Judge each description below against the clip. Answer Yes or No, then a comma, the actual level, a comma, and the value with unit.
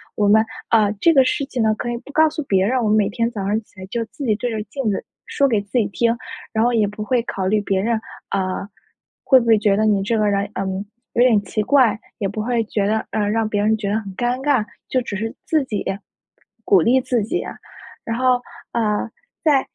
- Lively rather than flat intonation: No, average, 3.1 semitones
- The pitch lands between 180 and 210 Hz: No, high, 220 Hz